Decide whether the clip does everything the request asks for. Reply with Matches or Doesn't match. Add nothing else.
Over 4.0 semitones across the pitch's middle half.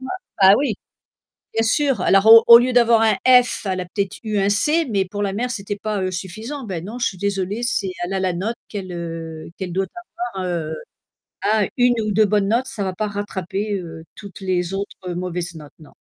Doesn't match